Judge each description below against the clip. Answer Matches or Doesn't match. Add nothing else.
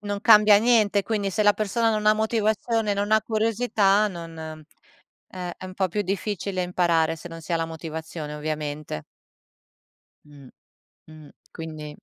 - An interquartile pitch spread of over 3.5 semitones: Matches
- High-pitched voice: Matches